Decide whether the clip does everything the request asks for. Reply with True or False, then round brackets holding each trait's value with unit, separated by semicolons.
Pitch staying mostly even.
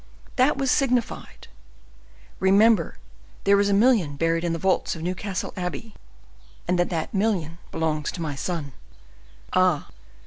False (4.0 semitones)